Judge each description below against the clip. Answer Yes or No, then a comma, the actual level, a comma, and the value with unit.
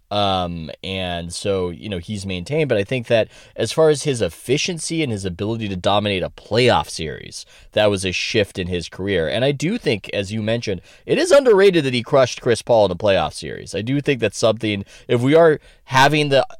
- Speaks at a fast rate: Yes, fast, 215 wpm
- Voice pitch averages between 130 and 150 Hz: No, low, 110 Hz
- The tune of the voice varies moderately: No, wide, 6.7 semitones